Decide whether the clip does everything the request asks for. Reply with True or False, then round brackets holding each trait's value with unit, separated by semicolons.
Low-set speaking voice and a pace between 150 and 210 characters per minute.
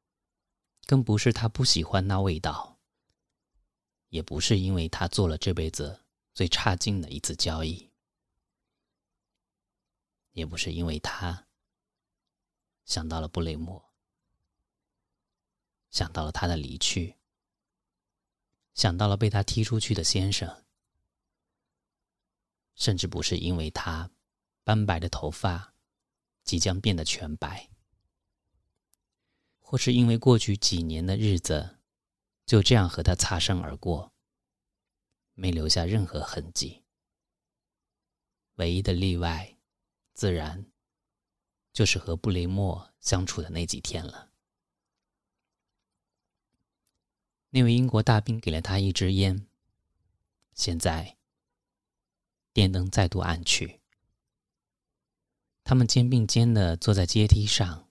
True (95 Hz; 160 characters per minute)